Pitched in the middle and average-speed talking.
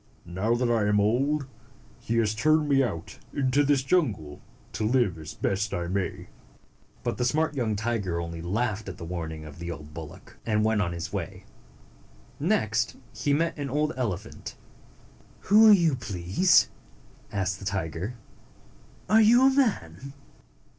No: low, 110 Hz; average, 160 wpm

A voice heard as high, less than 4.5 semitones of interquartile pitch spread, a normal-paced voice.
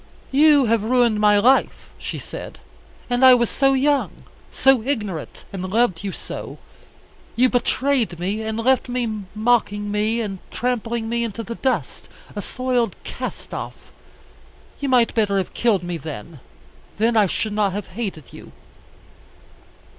Yes: high, 225 Hz; average, 3.3 semitones; average, 150 wpm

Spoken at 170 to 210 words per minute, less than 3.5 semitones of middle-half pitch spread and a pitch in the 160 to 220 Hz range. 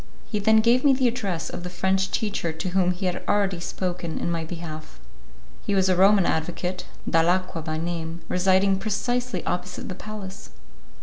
Yes: average, 175 wpm; average, 2.8 semitones; medium, 185 Hz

